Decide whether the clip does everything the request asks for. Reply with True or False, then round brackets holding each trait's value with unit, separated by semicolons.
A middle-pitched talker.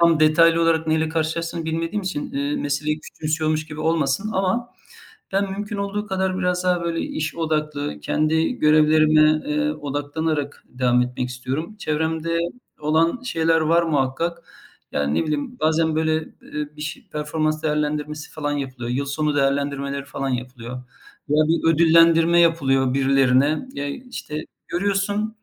True (155 Hz)